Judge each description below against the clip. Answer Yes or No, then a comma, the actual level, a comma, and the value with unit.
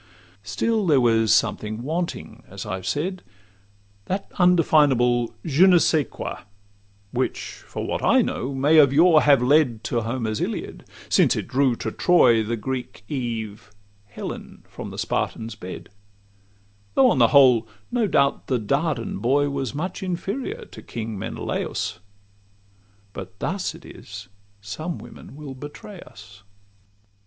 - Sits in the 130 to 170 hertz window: Yes, low, 135 Hz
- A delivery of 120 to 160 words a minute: Yes, average, 140 wpm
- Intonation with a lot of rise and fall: Yes, wide, 5.9 semitones